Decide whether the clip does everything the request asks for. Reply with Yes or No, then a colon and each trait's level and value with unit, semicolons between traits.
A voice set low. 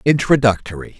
Yes: low, 115 Hz